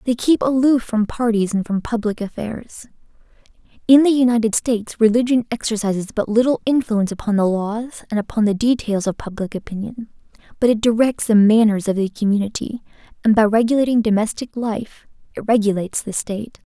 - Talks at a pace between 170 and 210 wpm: No, average, 160 wpm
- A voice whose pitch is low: No, high, 220 Hz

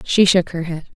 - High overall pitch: No, medium, 175 Hz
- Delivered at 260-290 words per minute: No, fast, 250 wpm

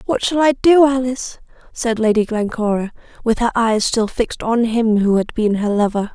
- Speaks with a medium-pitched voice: No, high, 230 Hz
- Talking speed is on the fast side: No, average, 195 wpm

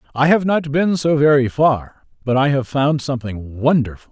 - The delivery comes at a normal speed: Yes, average, 190 wpm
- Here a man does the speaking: Yes, male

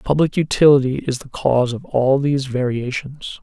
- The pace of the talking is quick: No, average, 160 wpm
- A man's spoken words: Yes, male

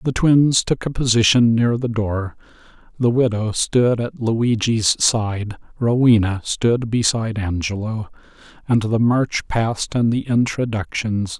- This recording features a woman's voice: No, male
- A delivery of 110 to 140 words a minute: Yes, slow, 135 wpm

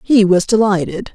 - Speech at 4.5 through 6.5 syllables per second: Yes, 4.8 syllables/s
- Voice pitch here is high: Yes, high, 200 Hz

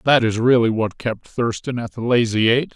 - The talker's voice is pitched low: Yes, low, 115 Hz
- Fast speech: Yes, fast, 220 wpm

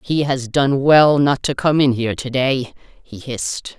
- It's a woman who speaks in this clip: Yes, female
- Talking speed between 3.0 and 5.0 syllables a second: Yes, 4.3 syllables/s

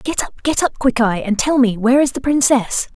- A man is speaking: No, female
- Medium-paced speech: No, fast, 240 wpm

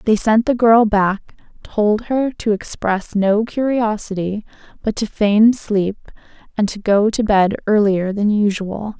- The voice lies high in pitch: Yes, high, 210 Hz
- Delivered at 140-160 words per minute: Yes, average, 155 wpm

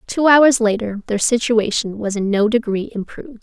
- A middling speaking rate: Yes, average, 175 wpm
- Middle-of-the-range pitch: No, high, 225 Hz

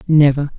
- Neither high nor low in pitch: Yes, medium, 145 Hz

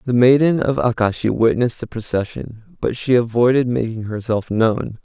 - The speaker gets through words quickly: No, average, 155 wpm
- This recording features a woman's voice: No, male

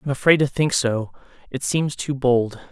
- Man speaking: Yes, male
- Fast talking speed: Yes, fast, 220 wpm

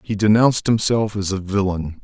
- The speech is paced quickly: No, average, 175 wpm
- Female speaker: No, male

